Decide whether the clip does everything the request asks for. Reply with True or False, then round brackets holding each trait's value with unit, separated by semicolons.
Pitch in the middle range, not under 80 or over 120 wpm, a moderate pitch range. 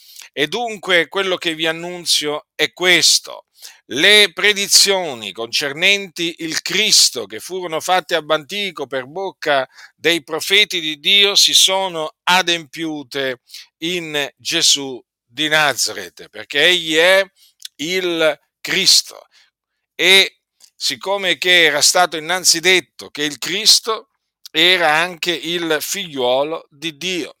True (170 Hz; 115 wpm; 3.6 semitones)